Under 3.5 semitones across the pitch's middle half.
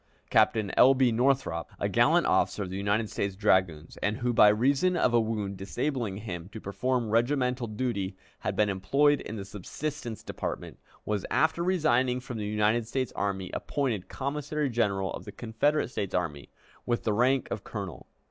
No: average, 4.5 semitones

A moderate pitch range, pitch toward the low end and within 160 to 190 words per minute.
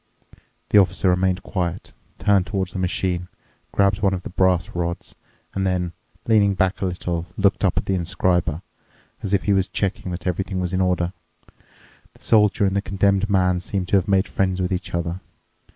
No: narrow, 1.6 semitones; very low, 95 Hz; average, 185 wpm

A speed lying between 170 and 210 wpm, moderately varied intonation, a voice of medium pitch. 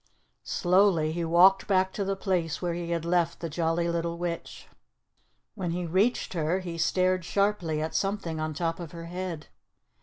No: average, 175 wpm; narrow, 2.0 semitones; medium, 170 Hz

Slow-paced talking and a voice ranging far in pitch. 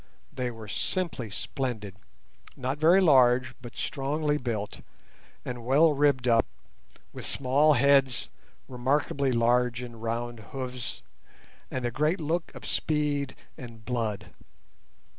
No: slow, 120 wpm; average, 3.3 semitones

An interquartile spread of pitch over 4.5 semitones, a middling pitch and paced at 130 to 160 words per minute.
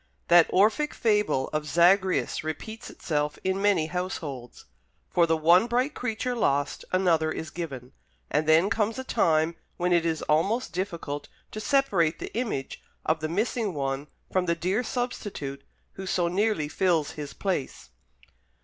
Yes: average, 4.9 semitones; medium, 175 Hz; average, 150 wpm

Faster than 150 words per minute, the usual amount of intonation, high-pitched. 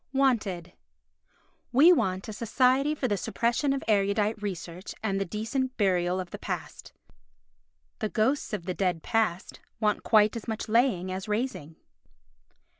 No: average, 145 wpm; average, 4.3 semitones; high, 210 Hz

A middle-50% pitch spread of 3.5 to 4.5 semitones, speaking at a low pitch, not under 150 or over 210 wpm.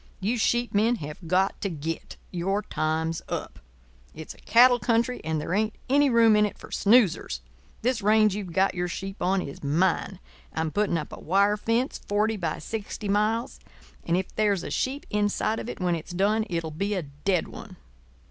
No: average, 4.2 semitones; high, 200 Hz; average, 190 wpm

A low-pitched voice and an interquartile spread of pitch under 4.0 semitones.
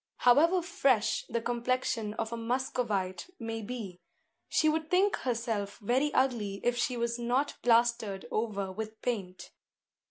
No: high, 235 Hz; average, 3.0 semitones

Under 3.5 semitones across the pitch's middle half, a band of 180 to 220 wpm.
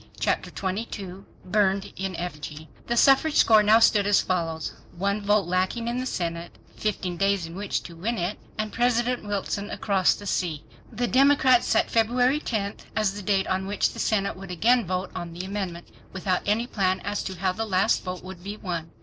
Yes: average, 3.0 semitones; average, 190 wpm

